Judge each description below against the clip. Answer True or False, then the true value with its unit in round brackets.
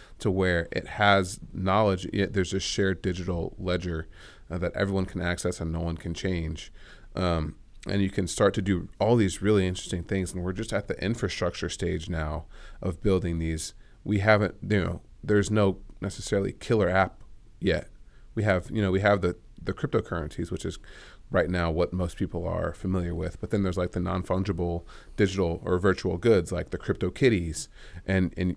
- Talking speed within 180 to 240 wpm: True (185 wpm)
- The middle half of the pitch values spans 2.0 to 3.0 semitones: True (2.4 semitones)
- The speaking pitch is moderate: False (95 Hz)